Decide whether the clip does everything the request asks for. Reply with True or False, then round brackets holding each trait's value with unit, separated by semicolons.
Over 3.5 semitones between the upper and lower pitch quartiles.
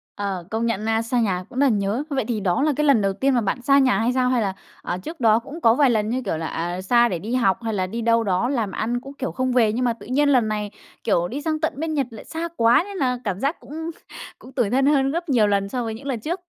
True (4.5 semitones)